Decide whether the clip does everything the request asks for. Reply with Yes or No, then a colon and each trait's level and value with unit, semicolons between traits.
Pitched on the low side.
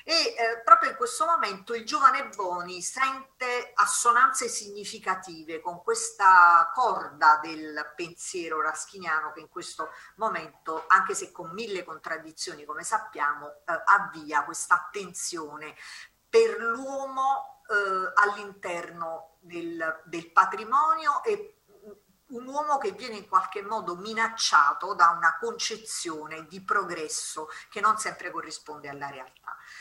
No: high, 195 Hz